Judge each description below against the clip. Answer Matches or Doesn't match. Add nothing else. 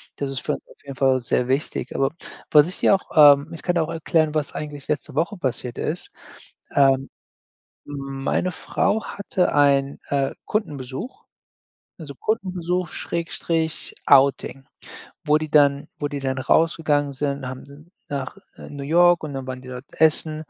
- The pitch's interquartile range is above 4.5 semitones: Doesn't match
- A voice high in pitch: Doesn't match